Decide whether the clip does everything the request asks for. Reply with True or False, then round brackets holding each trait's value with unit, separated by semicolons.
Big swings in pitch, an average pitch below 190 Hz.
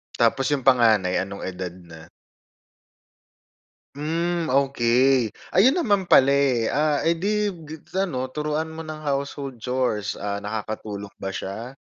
True (6.3 semitones; 135 Hz)